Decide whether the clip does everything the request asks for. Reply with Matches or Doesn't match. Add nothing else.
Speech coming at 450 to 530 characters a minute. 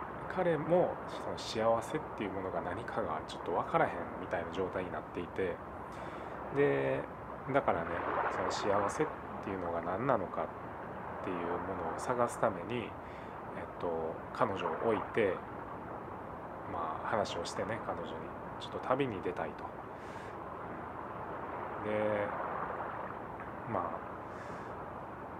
Doesn't match